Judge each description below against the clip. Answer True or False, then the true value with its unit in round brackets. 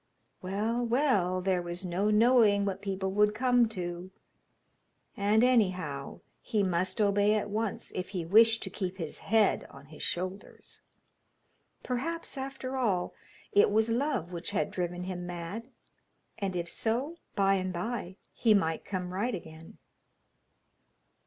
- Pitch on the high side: True (200 Hz)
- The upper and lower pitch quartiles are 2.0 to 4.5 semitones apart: True (3.9 semitones)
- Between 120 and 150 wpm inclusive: True (140 wpm)